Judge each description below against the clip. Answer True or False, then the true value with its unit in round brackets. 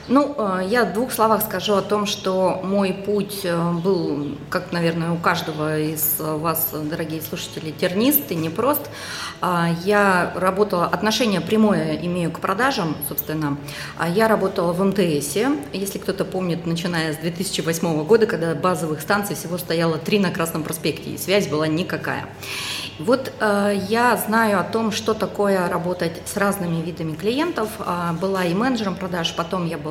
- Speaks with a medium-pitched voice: True (180 Hz)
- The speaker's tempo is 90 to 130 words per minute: False (150 wpm)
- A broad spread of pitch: False (3.7 semitones)